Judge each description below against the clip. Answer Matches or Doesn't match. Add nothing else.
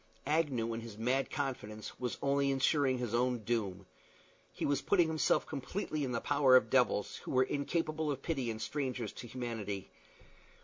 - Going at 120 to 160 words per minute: Doesn't match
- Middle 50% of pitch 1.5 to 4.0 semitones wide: Matches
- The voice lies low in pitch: Matches